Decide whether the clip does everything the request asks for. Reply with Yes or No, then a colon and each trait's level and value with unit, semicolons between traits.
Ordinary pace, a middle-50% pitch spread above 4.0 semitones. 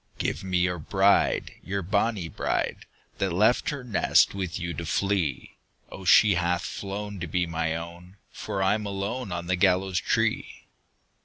No: average, 160 wpm; narrow, 2.6 semitones